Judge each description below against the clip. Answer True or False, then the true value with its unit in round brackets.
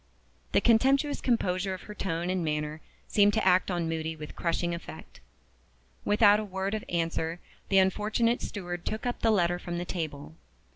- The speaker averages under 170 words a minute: False (175 wpm)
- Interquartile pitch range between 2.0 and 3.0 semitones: False (3.9 semitones)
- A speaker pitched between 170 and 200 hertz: True (185 Hz)